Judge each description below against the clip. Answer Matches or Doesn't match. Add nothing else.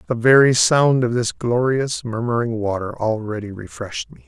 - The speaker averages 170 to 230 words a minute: Doesn't match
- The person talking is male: Matches